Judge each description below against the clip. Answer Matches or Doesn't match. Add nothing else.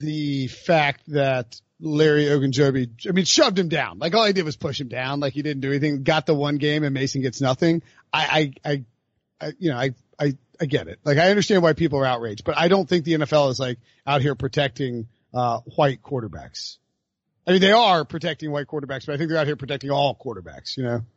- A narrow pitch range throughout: Doesn't match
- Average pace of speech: Doesn't match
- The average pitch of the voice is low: Doesn't match